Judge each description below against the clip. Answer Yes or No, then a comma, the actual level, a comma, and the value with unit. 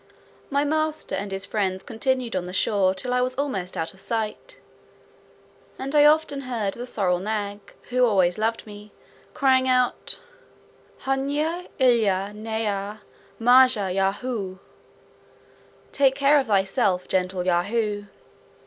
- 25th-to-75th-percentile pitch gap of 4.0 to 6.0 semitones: Yes, average, 5.1 semitones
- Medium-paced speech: No, slow, 130 wpm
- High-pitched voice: Yes, high, 220 Hz